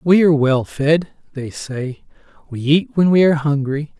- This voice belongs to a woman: No, male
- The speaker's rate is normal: Yes, average, 180 wpm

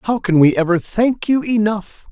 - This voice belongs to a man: Yes, male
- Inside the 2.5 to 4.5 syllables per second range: Yes, 4.4 syllables/s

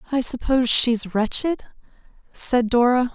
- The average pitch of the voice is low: No, high, 245 Hz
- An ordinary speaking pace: No, slow, 115 wpm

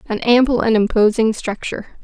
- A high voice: Yes, high, 225 Hz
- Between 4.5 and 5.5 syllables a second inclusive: No, 5.7 syllables/s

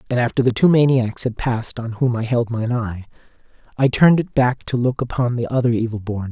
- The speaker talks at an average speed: No, fast, 230 wpm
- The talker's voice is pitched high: No, low, 120 Hz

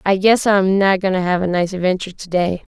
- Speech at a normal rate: No, fast, 260 wpm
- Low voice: No, high, 190 Hz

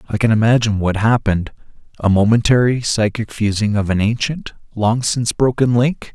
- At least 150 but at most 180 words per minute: Yes, average, 155 wpm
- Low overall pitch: Yes, low, 110 Hz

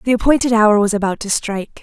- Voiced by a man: No, female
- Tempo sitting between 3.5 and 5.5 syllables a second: No, 6.4 syllables/s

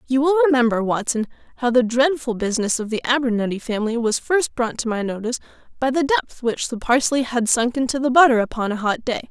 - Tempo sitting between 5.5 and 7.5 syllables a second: Yes, 6.0 syllables/s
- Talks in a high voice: Yes, high, 245 Hz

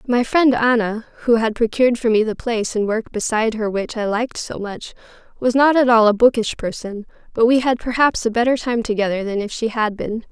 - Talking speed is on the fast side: Yes, fast, 225 wpm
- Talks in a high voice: Yes, high, 230 Hz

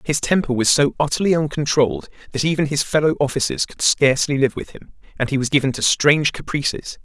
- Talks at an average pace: Yes, average, 195 wpm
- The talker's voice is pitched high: No, medium, 145 Hz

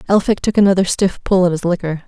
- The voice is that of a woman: Yes, female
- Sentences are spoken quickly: Yes, fast, 230 wpm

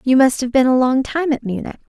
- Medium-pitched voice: No, very high, 260 Hz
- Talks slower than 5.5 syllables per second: No, 5.9 syllables/s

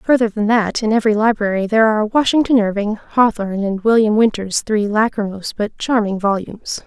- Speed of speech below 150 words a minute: No, average, 165 wpm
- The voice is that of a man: No, female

